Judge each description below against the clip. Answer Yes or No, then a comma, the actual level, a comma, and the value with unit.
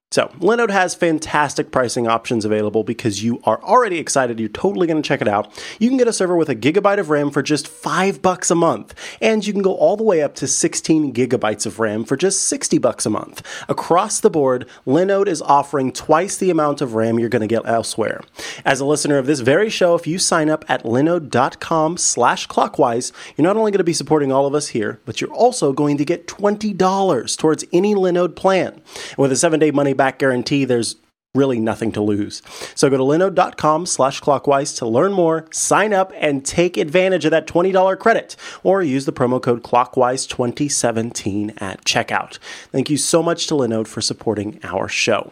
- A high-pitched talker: No, medium, 145 Hz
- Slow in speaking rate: No, average, 200 wpm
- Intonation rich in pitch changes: Yes, wide, 6.1 semitones